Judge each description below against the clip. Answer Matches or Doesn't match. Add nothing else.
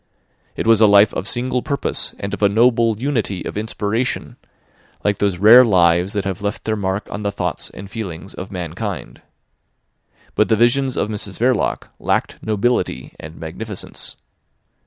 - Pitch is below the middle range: Matches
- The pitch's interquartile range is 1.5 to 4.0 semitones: Matches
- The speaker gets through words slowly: Doesn't match